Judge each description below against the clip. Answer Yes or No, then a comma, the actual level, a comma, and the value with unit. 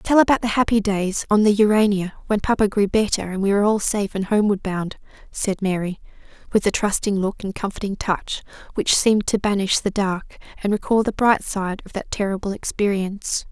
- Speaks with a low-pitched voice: No, high, 205 Hz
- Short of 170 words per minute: No, average, 195 wpm